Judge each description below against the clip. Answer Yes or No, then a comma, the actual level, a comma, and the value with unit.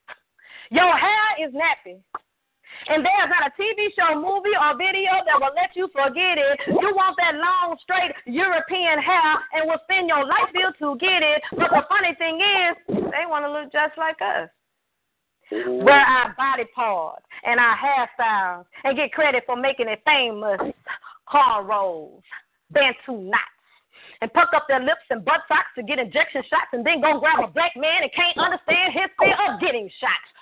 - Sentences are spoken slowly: No, average, 180 wpm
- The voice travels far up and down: No, average, 4.7 semitones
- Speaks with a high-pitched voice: Yes, very high, 310 Hz